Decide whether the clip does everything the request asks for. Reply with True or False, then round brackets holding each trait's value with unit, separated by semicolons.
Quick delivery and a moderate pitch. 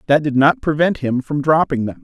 True (235 wpm; 150 Hz)